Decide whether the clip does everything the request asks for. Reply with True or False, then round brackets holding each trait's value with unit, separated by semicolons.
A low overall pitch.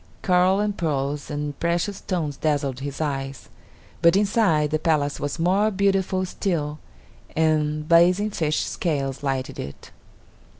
False (155 Hz)